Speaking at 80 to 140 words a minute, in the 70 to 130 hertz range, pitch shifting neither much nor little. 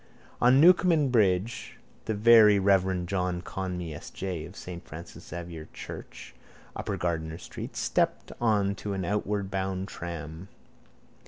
Yes: slow, 135 wpm; very low, 95 Hz; average, 3.2 semitones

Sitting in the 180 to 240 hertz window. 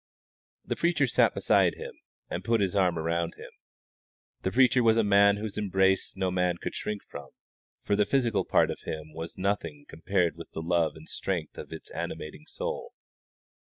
No: very low, 95 Hz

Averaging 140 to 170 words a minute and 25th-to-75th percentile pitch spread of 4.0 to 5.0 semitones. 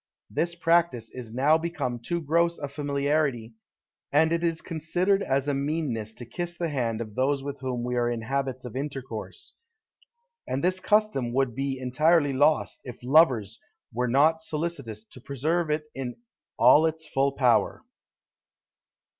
Yes: average, 155 wpm; average, 4.5 semitones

